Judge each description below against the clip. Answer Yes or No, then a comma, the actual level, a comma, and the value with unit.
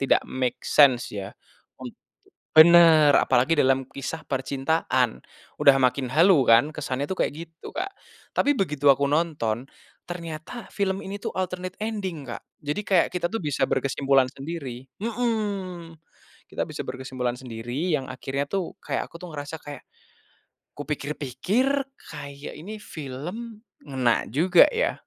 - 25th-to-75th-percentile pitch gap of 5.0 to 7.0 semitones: Yes, average, 5.3 semitones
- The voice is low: No, medium, 150 Hz